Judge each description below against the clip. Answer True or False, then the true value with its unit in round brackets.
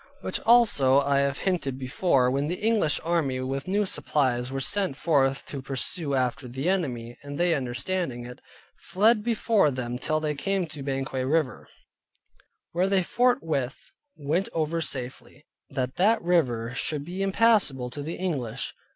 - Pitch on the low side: False (145 Hz)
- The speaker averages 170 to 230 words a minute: False (155 wpm)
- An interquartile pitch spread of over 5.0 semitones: True (5.5 semitones)